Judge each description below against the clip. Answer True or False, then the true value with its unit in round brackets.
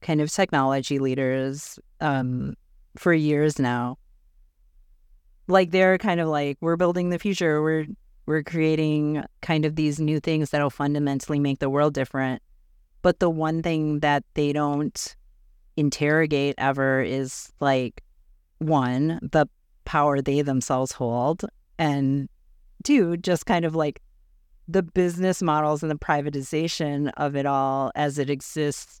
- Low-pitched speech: False (150 Hz)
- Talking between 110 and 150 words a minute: True (135 wpm)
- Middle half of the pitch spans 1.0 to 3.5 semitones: True (2.7 semitones)